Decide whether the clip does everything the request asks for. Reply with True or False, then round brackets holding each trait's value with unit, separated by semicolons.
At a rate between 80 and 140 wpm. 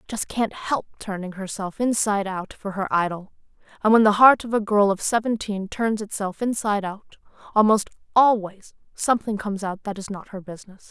False (180 wpm)